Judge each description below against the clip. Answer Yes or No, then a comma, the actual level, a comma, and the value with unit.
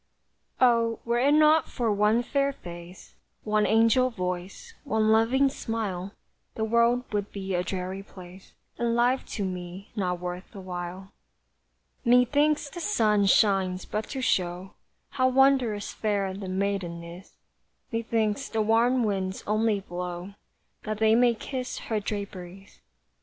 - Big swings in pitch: No, average, 4.0 semitones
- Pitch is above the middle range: Yes, high, 210 Hz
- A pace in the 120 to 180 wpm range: Yes, average, 140 wpm